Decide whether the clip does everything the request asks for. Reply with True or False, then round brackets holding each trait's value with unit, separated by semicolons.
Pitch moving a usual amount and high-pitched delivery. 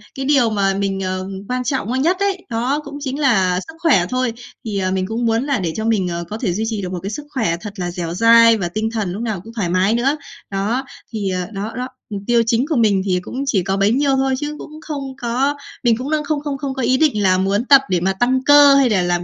False (5.7 semitones; 230 Hz)